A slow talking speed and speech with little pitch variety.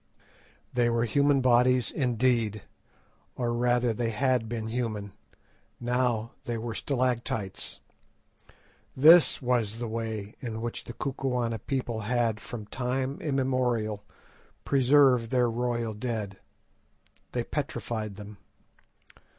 Yes: slow, 110 wpm; narrow, 2.3 semitones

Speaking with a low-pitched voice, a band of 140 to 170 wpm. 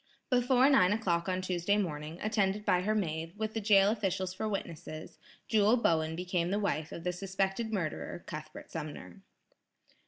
No: medium, 185 Hz; average, 160 wpm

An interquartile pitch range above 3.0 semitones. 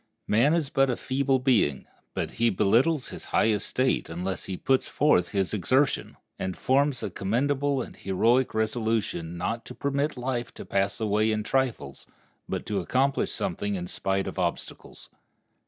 Yes: wide, 5.4 semitones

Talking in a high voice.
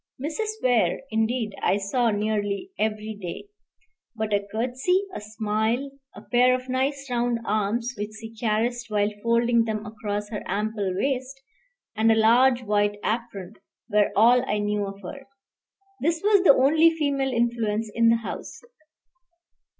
Yes: high, 230 Hz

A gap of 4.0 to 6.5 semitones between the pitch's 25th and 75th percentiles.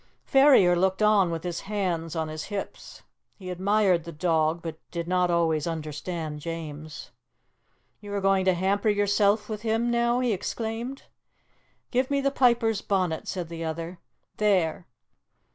Yes: average, 4.3 semitones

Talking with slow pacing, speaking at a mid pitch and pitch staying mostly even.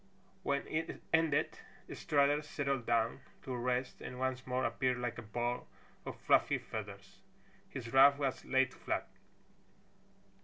No: slow, 130 wpm; low, 130 Hz; narrow, 2.3 semitones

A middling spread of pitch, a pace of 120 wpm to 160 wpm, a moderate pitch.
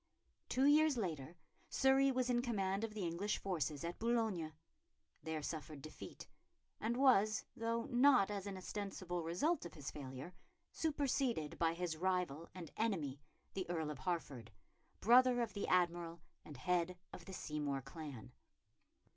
No: wide, 6.4 semitones; average, 145 wpm; medium, 180 Hz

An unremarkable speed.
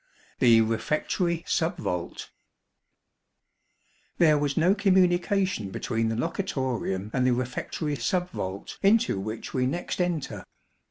No: slow, 115 wpm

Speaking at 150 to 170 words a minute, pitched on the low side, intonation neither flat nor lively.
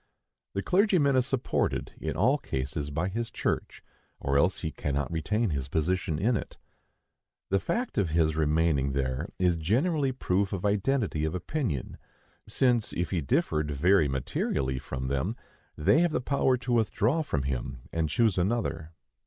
No: average, 160 wpm; very low, 90 Hz; wide, 8.1 semitones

